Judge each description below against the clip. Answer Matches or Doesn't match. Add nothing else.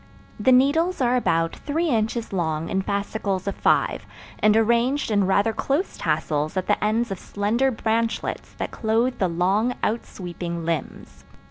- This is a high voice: Matches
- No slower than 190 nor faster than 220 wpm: Doesn't match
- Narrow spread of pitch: Doesn't match